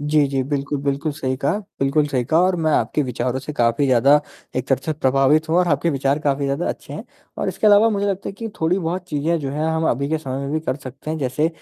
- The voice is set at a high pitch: No, medium, 145 Hz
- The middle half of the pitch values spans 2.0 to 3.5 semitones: Yes, average, 2.9 semitones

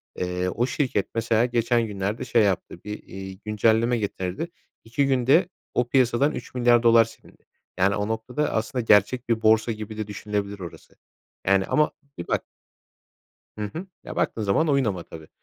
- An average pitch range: Yes, average, 3.3 semitones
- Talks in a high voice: No, low, 110 Hz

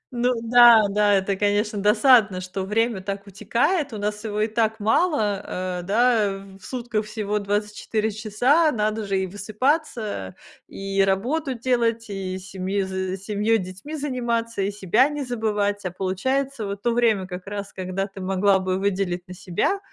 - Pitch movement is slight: No, average, 3.2 semitones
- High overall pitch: Yes, high, 210 Hz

